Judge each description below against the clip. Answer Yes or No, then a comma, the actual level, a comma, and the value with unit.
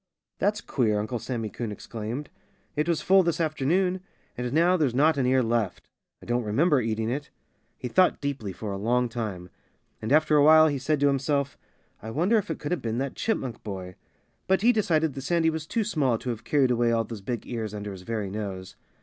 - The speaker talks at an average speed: No, fast, 215 wpm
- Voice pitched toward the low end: Yes, low, 130 Hz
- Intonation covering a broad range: Yes, wide, 5.8 semitones